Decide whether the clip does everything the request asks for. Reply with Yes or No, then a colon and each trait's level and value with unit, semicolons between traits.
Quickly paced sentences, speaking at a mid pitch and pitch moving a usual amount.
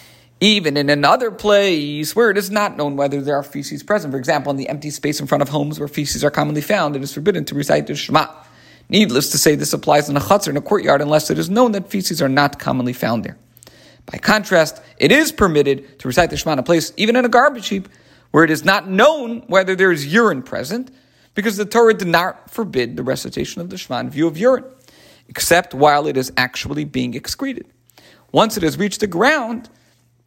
No: fast, 225 wpm; medium, 165 Hz; wide, 6.5 semitones